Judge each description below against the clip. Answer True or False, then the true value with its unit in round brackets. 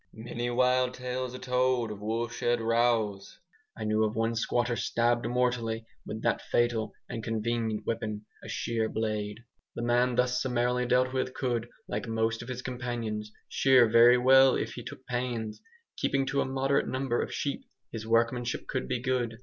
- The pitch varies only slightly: True (2.0 semitones)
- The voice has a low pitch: True (120 Hz)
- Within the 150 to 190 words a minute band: True (170 wpm)